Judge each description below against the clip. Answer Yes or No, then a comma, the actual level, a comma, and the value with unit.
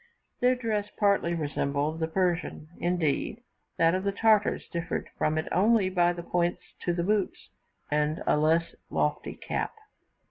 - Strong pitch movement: No, average, 3.8 semitones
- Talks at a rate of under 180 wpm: Yes, average, 145 wpm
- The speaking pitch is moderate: Yes, medium, 175 Hz